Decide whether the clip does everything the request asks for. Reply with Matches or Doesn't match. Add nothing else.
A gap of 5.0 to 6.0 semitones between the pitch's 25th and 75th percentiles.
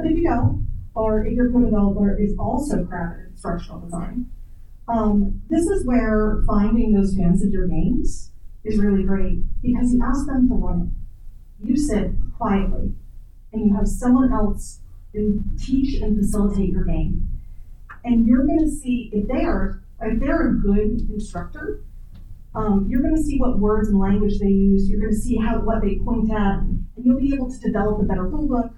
Doesn't match